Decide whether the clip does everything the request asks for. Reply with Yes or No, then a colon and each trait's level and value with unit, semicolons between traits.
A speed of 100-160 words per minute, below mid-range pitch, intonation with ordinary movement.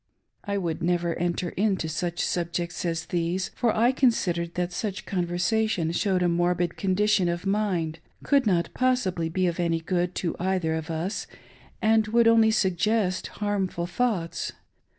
No: average, 155 wpm; medium, 180 Hz; average, 3.5 semitones